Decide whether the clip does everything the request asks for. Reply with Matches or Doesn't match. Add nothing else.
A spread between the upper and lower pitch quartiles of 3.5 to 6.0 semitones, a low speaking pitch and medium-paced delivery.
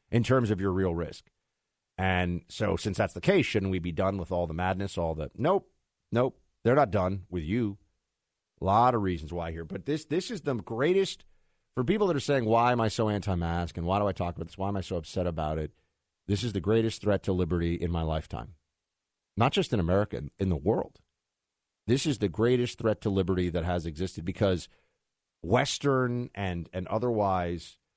Doesn't match